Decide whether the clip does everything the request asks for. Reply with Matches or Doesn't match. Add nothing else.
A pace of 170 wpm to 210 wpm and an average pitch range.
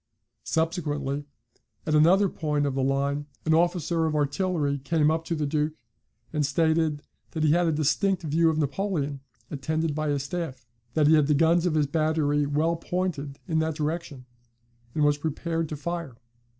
Doesn't match